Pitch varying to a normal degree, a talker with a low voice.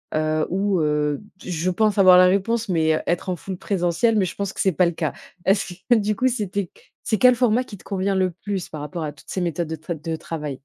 No: average, 3.8 semitones; medium, 185 Hz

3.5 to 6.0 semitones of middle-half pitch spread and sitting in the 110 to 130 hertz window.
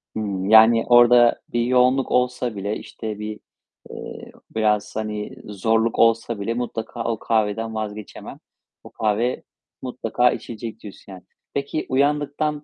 No: narrow, 2.5 semitones; low, 115 Hz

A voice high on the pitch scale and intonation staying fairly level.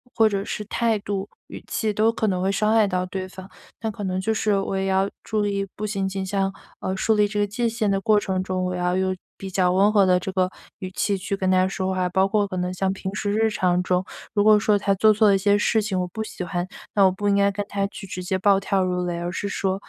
Yes: high, 195 Hz; narrow, 1.9 semitones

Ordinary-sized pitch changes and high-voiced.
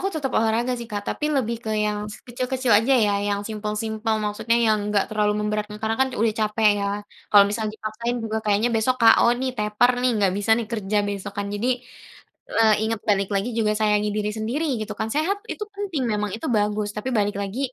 No: narrow, 2.3 semitones; high, 220 Hz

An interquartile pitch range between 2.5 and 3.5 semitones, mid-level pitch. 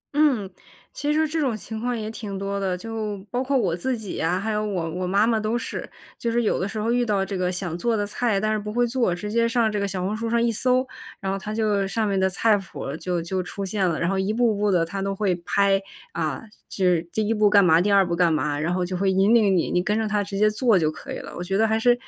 No: average, 3.2 semitones; high, 205 Hz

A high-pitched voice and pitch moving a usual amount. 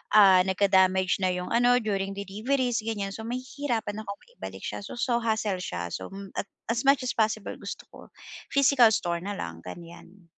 Yes: high, 205 Hz; average, 4.0 semitones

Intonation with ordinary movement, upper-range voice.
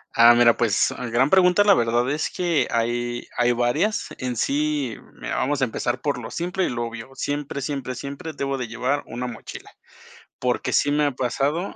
No: average, 3.5 semitones; low, 130 Hz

